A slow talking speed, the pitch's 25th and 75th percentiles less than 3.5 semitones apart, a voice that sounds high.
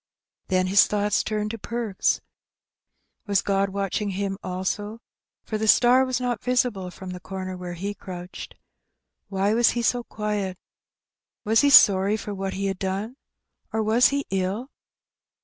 No: average, 155 wpm; average, 2.7 semitones; high, 205 Hz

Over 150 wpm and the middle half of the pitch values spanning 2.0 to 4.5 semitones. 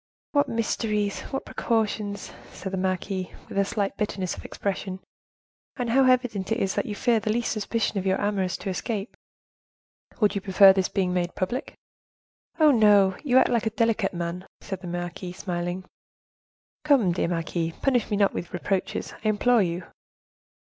Yes: average, 170 wpm; average, 3.4 semitones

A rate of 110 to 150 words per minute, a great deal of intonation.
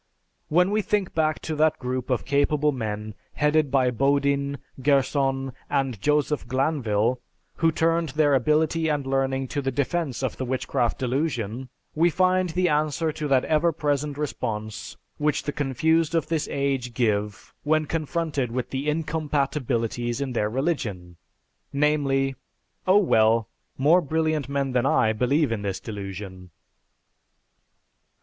No: average, 140 wpm; average, 3.7 semitones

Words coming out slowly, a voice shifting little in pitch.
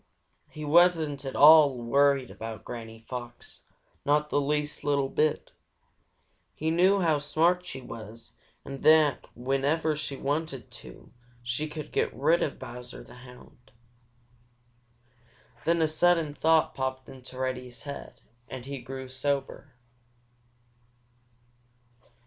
No: slow, 120 wpm; average, 3.3 semitones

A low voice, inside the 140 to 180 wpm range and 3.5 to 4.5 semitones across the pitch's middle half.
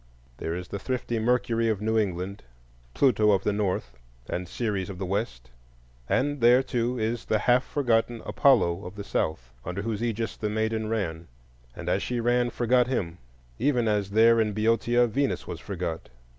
Yes: low, 110 Hz; average, 175 wpm; average, 4.0 semitones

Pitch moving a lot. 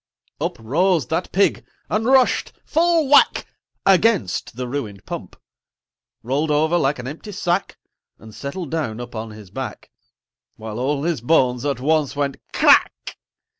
Yes: wide, 6.5 semitones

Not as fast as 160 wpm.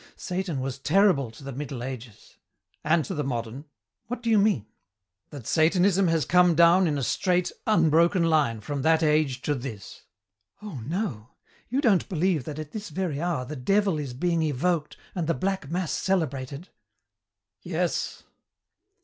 No: average, 165 wpm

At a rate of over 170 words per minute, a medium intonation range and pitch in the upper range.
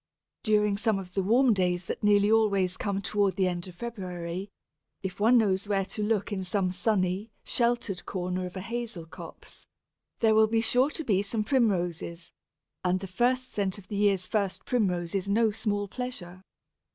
Yes: average, 180 wpm; average, 3.2 semitones; high, 200 Hz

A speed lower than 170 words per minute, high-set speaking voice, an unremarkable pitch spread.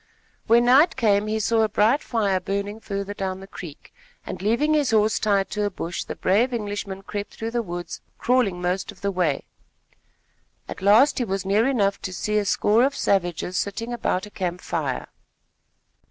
No: average, 185 wpm; high, 205 Hz; average, 3.1 semitones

